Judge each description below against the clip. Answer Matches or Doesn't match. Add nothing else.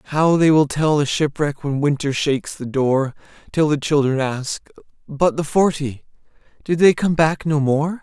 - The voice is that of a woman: Doesn't match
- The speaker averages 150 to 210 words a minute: Matches